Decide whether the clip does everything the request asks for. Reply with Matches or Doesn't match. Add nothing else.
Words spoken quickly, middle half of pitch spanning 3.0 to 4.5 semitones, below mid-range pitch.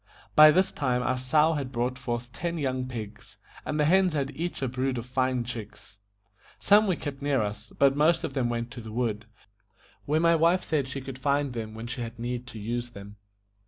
Matches